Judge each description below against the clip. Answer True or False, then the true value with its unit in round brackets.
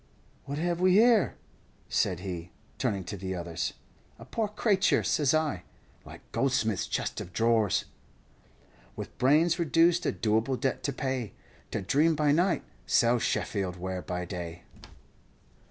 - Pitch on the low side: True (130 Hz)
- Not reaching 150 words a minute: True (140 wpm)